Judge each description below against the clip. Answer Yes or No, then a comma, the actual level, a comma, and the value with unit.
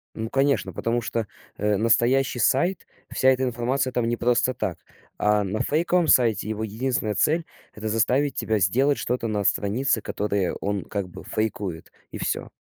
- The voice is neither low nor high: No, low, 115 Hz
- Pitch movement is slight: No, average, 3.8 semitones